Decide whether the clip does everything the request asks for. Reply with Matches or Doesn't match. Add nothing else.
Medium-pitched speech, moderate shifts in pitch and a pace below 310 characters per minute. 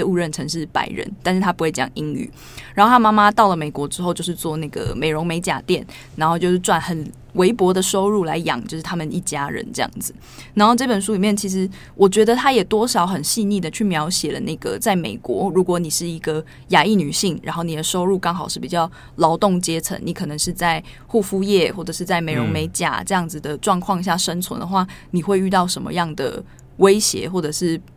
Doesn't match